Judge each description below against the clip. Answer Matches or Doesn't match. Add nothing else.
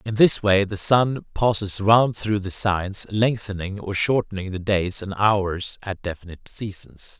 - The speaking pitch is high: Doesn't match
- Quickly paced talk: Doesn't match